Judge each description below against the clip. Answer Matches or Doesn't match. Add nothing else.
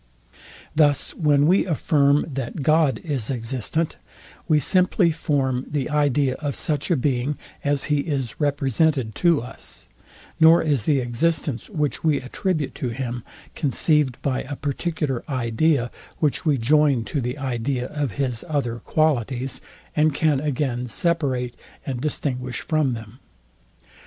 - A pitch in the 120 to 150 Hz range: Matches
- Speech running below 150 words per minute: Matches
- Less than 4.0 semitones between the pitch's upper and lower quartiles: Matches